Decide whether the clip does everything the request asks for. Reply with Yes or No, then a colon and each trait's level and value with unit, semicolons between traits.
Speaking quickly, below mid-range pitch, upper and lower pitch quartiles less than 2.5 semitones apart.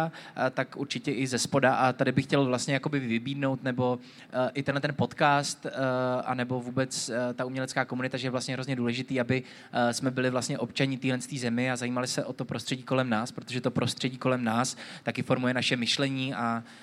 Yes: fast, 210 wpm; low, 130 Hz; narrow, 1.3 semitones